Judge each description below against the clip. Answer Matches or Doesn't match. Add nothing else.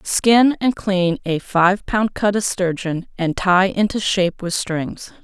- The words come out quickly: Doesn't match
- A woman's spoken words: Matches